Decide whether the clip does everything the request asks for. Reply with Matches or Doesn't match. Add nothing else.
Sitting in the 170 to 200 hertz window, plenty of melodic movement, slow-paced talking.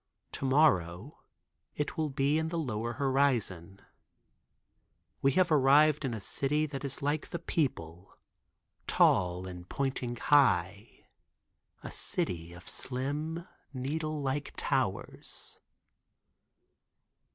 Doesn't match